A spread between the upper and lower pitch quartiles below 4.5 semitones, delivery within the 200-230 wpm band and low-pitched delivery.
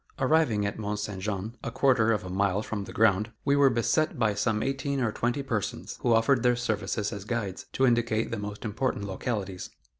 Yes: average, 3.2 semitones; fast, 205 wpm; low, 110 Hz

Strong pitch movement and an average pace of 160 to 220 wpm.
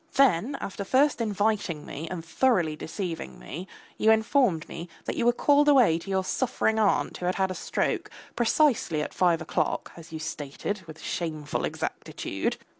Yes: wide, 6.0 semitones; average, 170 wpm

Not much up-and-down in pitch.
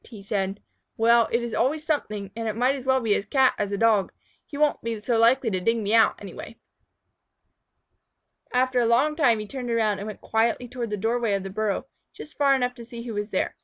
No: average, 3.0 semitones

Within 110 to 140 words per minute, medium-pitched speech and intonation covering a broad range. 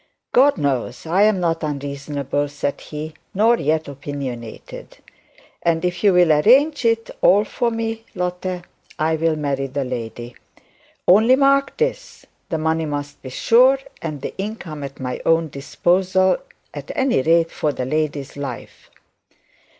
Yes: slow, 135 wpm; medium, 160 Hz; wide, 5.9 semitones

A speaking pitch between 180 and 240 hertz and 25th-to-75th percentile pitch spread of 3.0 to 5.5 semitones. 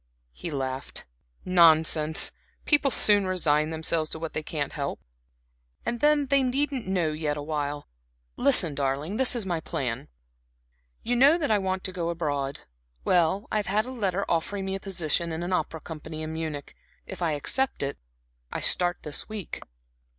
No: medium, 170 Hz; average, 5.0 semitones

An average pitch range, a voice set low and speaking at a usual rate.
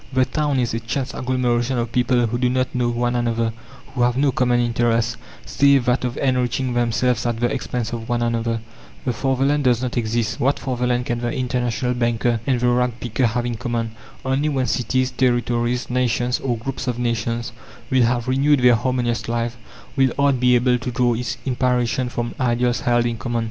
No: narrow, 1.2 semitones; low, 120 Hz; average, 195 wpm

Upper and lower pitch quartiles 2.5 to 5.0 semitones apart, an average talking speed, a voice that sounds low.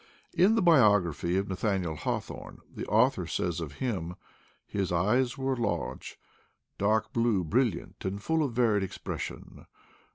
No: wide, 5.5 semitones; average, 150 wpm; low, 105 Hz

